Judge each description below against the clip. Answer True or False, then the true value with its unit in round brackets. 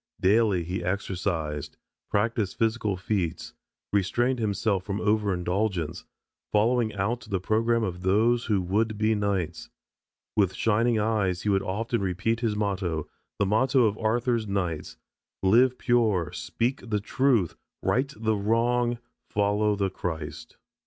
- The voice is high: False (105 Hz)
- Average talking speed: False (130 wpm)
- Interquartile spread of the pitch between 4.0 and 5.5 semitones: False (3.3 semitones)